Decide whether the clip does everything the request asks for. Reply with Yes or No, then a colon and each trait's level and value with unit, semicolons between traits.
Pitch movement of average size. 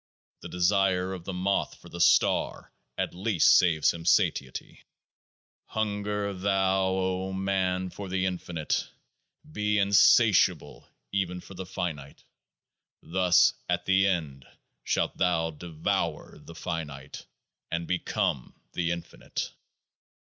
No: narrow, 2.3 semitones